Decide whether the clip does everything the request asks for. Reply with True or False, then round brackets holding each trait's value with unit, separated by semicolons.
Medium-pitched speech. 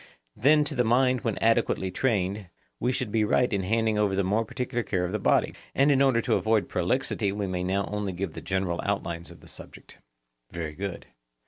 False (105 Hz)